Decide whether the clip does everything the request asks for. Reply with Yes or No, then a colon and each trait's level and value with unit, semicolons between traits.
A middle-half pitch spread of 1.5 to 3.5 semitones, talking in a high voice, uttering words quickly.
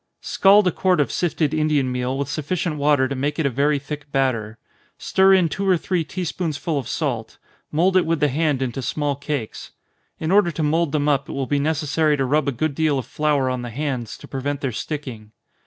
No: average, 3.0 semitones; medium, 145 Hz; fast, 225 wpm